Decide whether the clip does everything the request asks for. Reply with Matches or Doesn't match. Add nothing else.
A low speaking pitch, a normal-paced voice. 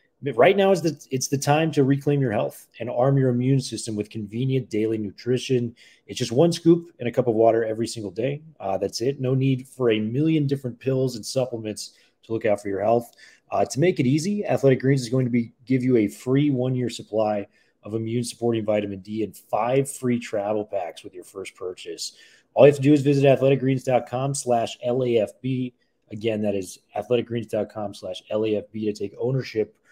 Matches